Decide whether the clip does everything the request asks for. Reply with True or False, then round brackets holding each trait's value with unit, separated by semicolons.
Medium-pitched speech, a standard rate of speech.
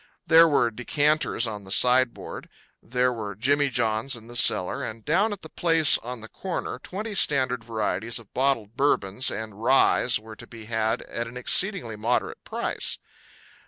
False (120 Hz; 165 wpm)